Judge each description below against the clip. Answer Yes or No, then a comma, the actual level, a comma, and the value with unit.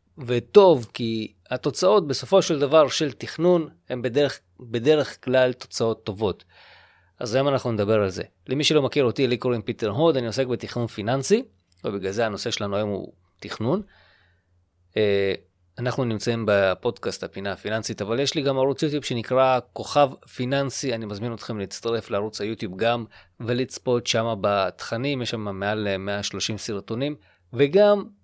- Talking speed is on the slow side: No, average, 145 wpm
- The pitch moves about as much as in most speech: Yes, average, 4.5 semitones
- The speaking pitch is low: Yes, low, 120 Hz